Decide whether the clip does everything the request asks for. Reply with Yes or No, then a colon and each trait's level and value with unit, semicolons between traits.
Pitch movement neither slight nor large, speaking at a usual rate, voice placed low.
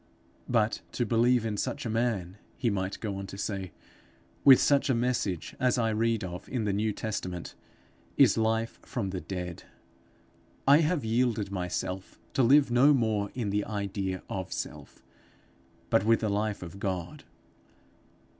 Yes: average, 3.7 semitones; average, 160 wpm; low, 110 Hz